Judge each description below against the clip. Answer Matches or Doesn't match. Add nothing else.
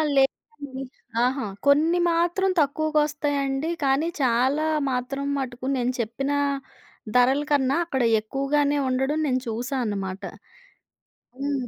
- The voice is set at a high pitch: Matches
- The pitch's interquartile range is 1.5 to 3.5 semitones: Matches